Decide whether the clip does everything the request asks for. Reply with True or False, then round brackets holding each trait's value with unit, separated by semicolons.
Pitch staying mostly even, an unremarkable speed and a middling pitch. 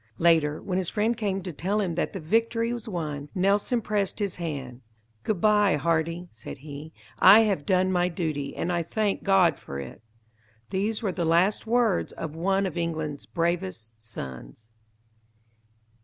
False (4.7 semitones; 165 wpm; 175 Hz)